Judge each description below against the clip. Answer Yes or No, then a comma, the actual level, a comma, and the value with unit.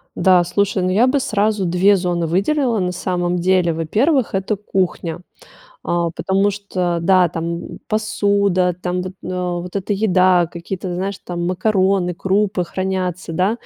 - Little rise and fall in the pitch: Yes, narrow, 2.2 semitones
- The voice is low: No, medium, 185 Hz